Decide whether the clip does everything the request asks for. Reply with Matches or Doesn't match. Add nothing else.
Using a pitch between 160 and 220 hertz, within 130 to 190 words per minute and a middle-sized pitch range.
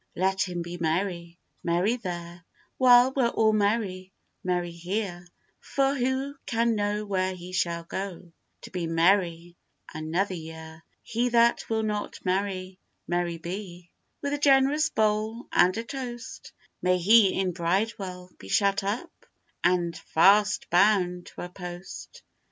Matches